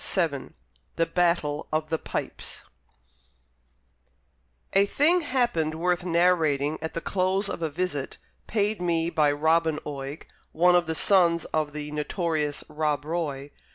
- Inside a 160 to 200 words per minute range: No, slow, 135 wpm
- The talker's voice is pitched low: No, medium, 165 Hz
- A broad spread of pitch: No, average, 2.9 semitones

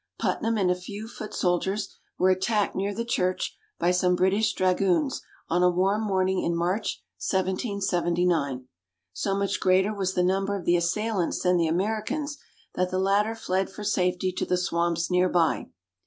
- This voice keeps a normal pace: Yes, average, 170 wpm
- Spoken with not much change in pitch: Yes, narrow, 2.2 semitones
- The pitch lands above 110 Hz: Yes, medium, 185 Hz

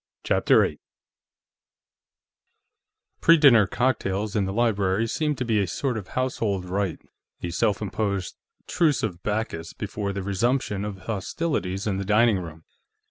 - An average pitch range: Yes, average, 3.5 semitones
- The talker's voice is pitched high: No, low, 105 Hz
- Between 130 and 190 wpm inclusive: Yes, average, 140 wpm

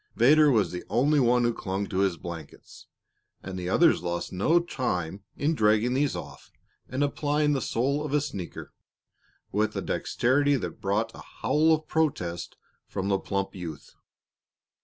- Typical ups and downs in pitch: No, wide, 7.1 semitones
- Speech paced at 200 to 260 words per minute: No, average, 160 wpm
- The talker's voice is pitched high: No, low, 115 Hz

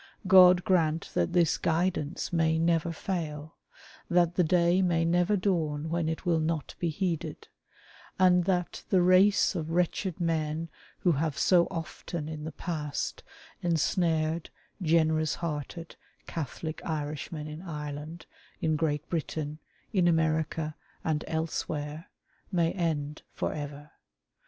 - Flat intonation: Yes, narrow, 2.2 semitones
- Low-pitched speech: No, medium, 165 Hz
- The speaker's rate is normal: No, slow, 125 wpm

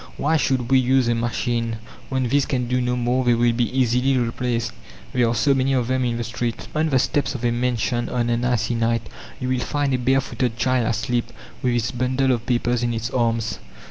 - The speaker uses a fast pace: Yes, fast, 225 wpm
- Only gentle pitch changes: Yes, narrow, 1.7 semitones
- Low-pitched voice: Yes, low, 125 Hz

